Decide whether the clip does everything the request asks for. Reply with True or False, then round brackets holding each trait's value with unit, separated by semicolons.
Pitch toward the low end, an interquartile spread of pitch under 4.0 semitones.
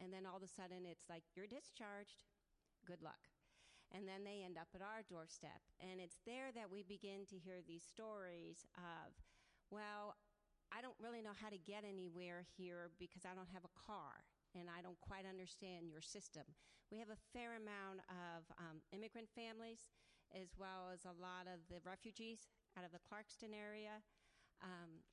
False (185 Hz; 3.0 semitones)